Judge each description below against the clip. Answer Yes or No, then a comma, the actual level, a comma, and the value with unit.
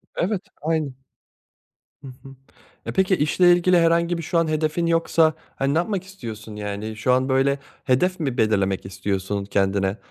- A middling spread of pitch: No, wide, 7.9 semitones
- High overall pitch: No, medium, 140 Hz